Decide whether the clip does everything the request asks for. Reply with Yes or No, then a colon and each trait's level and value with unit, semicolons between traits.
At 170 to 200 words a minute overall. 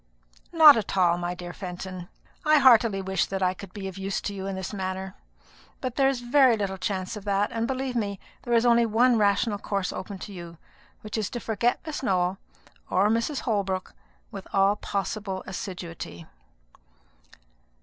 Yes: average, 180 wpm